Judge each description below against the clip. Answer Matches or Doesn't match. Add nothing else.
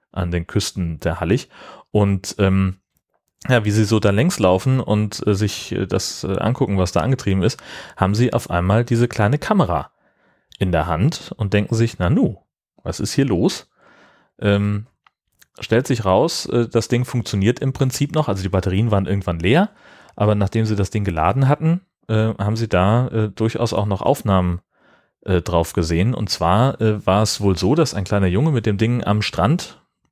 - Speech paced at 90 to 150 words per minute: Doesn't match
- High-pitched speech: Doesn't match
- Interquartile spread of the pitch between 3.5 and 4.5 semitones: Matches